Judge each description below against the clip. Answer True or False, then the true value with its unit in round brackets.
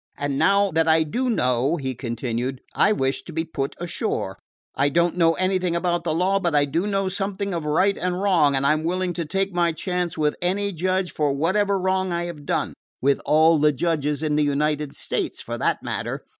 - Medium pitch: True (165 Hz)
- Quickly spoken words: True (210 wpm)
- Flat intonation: False (4.0 semitones)